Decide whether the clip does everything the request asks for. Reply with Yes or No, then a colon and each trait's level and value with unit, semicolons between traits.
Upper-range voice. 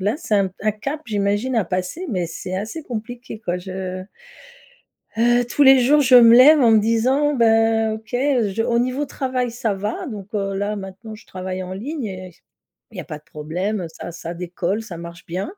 Yes: high, 215 Hz